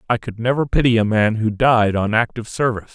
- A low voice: Yes, low, 115 Hz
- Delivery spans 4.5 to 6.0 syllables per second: No, 6.2 syllables/s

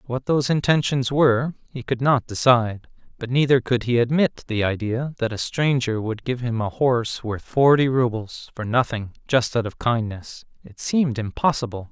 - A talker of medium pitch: No, low, 125 Hz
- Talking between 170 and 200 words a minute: Yes, average, 175 wpm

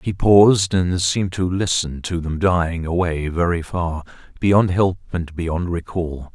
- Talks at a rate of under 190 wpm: Yes, average, 150 wpm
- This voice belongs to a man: Yes, male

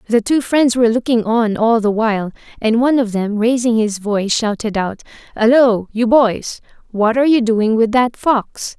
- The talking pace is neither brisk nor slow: Yes, average, 190 wpm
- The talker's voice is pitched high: Yes, high, 230 Hz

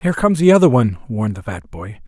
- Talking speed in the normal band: No, fast, 260 wpm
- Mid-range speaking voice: No, low, 130 Hz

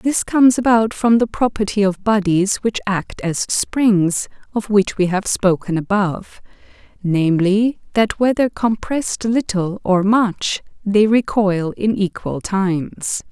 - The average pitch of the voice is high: Yes, high, 205 Hz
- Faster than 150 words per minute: No, slow, 135 wpm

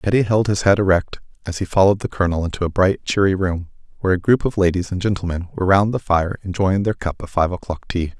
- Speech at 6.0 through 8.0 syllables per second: Yes, 6.4 syllables/s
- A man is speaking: Yes, male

